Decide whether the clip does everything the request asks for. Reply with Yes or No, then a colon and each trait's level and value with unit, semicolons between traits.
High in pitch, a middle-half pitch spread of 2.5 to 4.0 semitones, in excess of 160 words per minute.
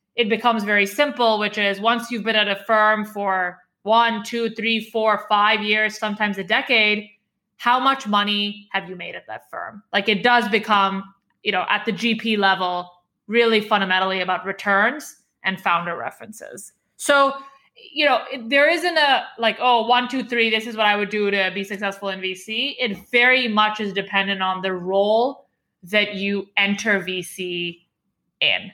Yes: high, 210 Hz; average, 2.9 semitones; average, 175 wpm